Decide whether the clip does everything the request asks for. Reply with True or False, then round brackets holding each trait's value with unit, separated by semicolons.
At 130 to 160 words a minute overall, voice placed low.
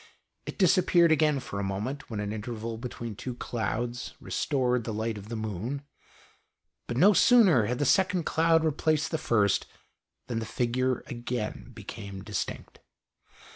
True (150 wpm; 120 Hz)